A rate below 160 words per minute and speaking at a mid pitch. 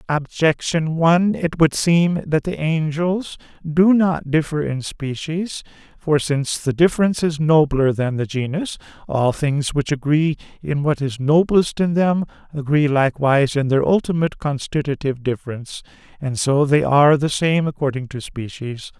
Yes: average, 150 wpm; medium, 150 Hz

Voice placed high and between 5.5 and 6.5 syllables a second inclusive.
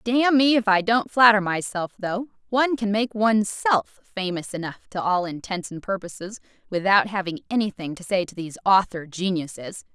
No: high, 200 Hz; 5.1 syllables/s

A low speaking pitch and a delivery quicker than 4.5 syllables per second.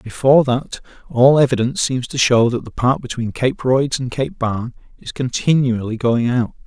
Yes: low, 125 Hz; 5.0 syllables/s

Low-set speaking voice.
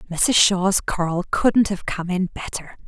No: high, 190 Hz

